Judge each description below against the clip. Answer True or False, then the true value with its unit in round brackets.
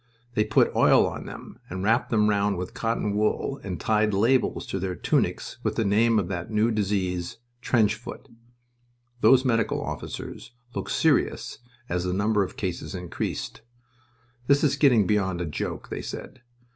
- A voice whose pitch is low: True (105 Hz)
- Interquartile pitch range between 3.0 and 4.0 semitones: True (3.5 semitones)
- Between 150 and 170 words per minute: True (165 wpm)